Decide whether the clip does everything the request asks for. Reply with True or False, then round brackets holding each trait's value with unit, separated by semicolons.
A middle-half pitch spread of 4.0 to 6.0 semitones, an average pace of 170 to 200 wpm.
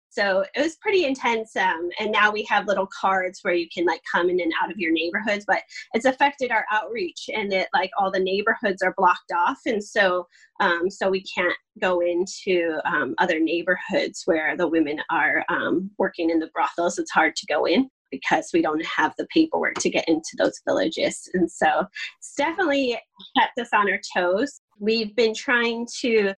True (4.9 semitones; 195 wpm)